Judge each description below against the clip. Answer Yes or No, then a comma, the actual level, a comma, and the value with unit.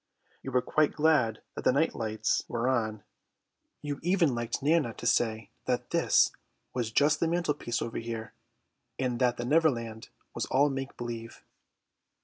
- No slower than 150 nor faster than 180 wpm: Yes, average, 155 wpm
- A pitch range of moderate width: Yes, average, 4.2 semitones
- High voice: No, low, 125 Hz